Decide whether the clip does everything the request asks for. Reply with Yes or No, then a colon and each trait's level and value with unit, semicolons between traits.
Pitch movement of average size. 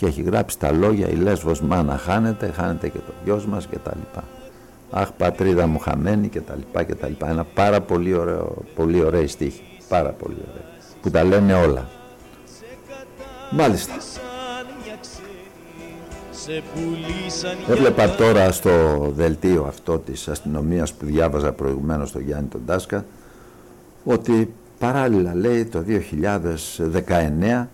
No: wide, 6.0 semitones